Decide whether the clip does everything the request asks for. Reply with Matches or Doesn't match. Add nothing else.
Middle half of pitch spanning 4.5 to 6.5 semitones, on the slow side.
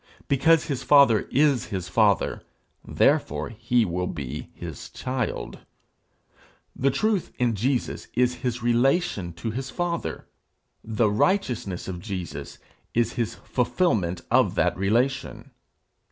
Matches